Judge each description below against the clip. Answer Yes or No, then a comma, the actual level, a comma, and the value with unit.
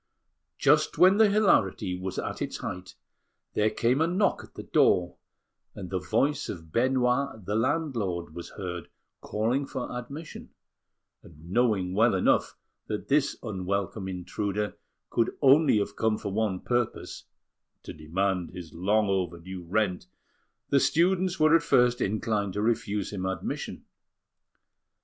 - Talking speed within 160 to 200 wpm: No, average, 140 wpm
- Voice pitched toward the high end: No, low, 105 Hz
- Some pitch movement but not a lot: No, wide, 5.9 semitones